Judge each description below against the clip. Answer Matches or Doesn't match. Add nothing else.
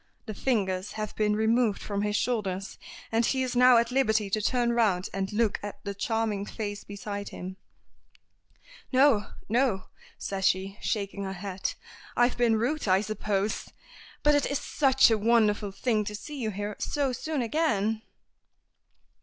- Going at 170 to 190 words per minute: Doesn't match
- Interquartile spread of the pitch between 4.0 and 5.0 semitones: Doesn't match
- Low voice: Doesn't match